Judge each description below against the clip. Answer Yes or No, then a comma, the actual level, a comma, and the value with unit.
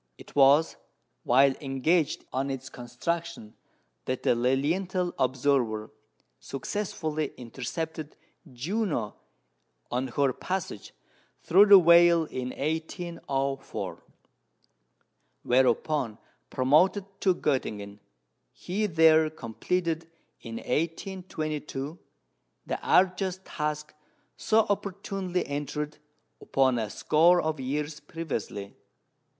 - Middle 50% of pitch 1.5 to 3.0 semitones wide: No, average, 4.8 semitones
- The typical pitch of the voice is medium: Yes, medium, 150 Hz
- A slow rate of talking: Yes, slow, 90 wpm